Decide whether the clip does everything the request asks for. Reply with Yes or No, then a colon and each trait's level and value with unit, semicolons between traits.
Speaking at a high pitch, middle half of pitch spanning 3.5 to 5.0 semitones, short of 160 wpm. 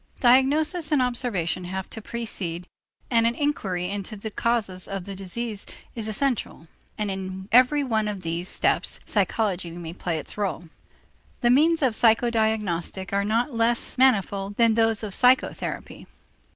Yes: high, 215 Hz; average, 4.1 semitones; average, 150 wpm